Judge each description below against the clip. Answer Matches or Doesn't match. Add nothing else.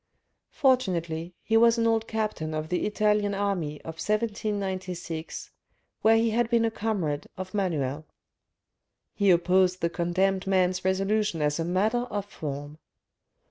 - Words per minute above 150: Doesn't match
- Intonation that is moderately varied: Matches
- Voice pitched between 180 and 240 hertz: Matches